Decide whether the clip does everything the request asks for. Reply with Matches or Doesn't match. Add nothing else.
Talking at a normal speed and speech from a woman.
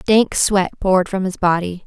Matches